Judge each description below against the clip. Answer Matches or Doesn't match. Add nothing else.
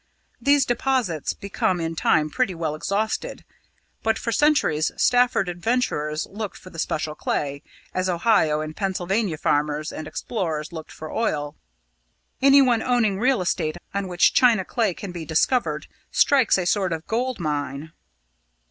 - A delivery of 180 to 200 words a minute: Doesn't match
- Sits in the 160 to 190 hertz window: Matches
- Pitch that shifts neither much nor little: Doesn't match